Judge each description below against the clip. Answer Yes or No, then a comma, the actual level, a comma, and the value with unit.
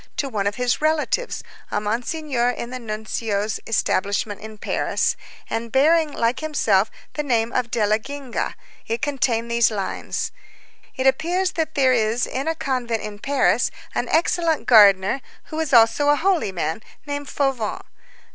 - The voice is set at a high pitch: Yes, high, 245 Hz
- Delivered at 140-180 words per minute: Yes, average, 155 wpm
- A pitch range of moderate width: Yes, average, 5.0 semitones